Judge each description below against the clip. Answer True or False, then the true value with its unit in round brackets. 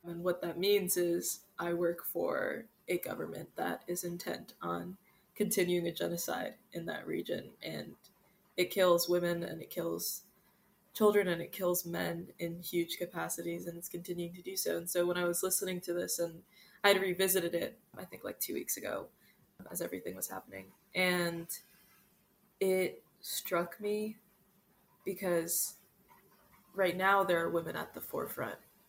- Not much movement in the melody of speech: True (2.2 semitones)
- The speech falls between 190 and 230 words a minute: False (160 wpm)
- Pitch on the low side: False (180 Hz)